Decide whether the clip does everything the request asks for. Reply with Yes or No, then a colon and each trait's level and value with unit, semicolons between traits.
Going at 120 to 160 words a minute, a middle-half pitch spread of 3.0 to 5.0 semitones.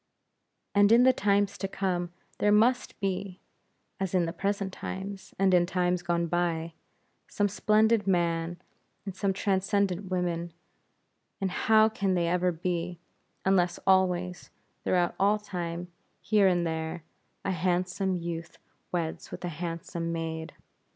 No: average, 140 wpm; narrow, 2.4 semitones